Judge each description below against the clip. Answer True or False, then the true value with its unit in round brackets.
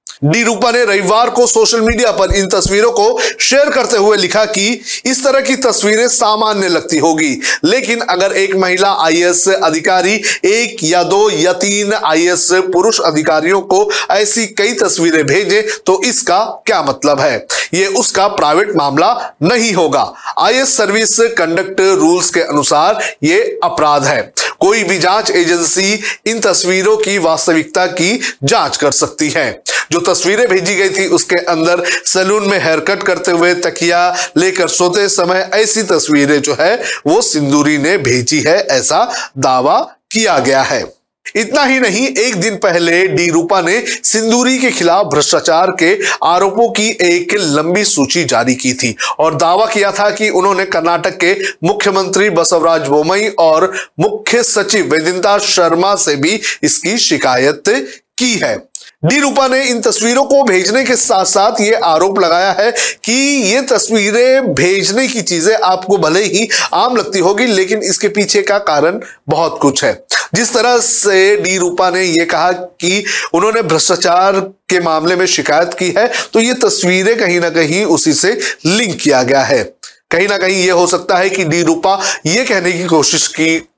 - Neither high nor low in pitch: False (195 Hz)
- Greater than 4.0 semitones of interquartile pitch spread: True (4.5 semitones)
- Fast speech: False (165 wpm)